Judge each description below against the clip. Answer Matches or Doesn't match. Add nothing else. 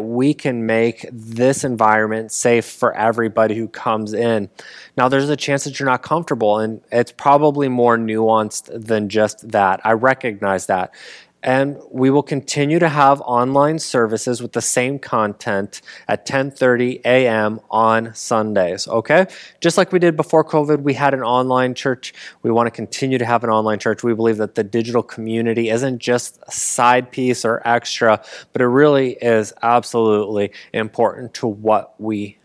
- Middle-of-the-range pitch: Doesn't match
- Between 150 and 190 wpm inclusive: Matches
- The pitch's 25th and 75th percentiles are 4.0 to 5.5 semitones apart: Doesn't match